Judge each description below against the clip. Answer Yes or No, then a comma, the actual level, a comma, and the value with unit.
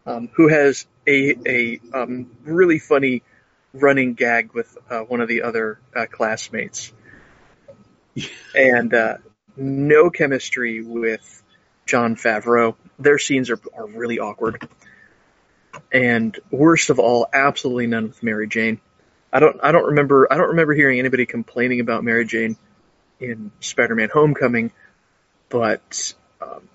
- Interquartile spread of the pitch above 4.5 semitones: No, average, 3.1 semitones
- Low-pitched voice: Yes, low, 120 Hz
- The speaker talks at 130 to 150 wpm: Yes, slow, 135 wpm